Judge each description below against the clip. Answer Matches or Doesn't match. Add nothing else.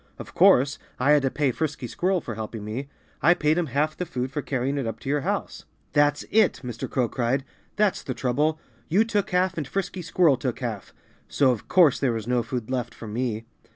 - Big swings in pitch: Doesn't match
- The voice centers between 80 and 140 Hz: Matches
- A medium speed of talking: Doesn't match